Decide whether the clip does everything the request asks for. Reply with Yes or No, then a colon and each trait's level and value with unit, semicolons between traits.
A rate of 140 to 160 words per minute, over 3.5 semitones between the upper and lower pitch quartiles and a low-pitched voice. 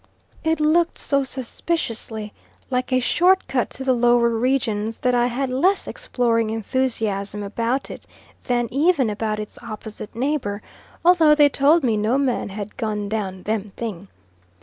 No: average, 150 wpm; average, 4.1 semitones; high, 240 Hz